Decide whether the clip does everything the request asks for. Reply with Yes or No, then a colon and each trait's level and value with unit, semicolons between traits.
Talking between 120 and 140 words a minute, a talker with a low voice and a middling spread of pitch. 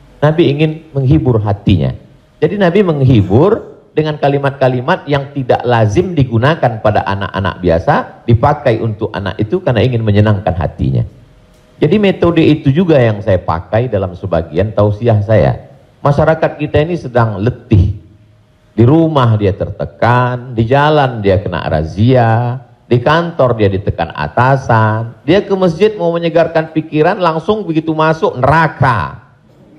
No: average, 130 wpm; low, 125 Hz; wide, 6.5 semitones